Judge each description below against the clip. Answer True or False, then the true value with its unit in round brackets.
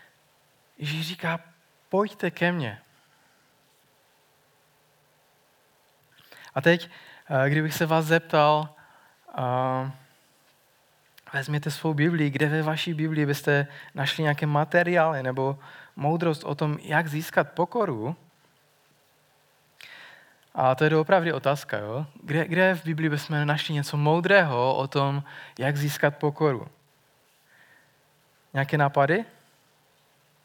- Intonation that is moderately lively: False (2.2 semitones)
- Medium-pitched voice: True (150 Hz)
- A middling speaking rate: False (100 wpm)